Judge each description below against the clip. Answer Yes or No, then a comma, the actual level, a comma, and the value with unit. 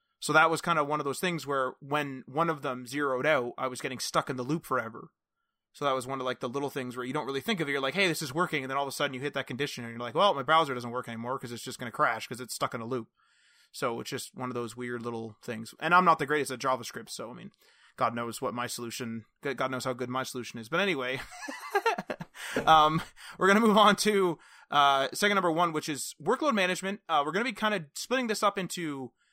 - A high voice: No, medium, 140 Hz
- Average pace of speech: No, fast, 280 wpm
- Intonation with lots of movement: No, average, 4.7 semitones